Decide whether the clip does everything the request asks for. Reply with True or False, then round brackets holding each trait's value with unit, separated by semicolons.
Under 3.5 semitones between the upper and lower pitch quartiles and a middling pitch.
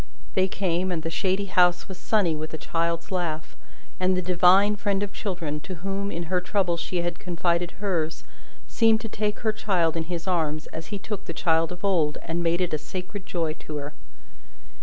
True (2.8 semitones; 180 Hz)